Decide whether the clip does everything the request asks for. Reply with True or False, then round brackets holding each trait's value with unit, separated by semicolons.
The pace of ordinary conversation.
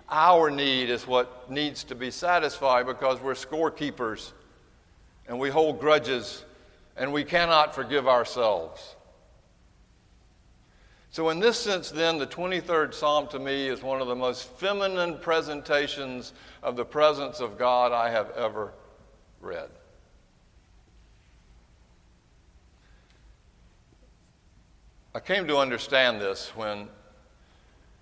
False (110 wpm)